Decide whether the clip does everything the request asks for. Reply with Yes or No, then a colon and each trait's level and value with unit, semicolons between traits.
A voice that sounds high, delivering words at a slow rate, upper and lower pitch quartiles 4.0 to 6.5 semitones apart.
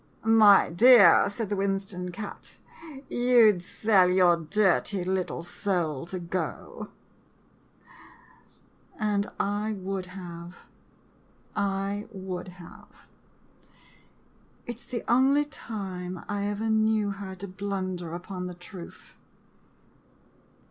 No: high, 195 Hz; slow, 115 wpm; average, 2.7 semitones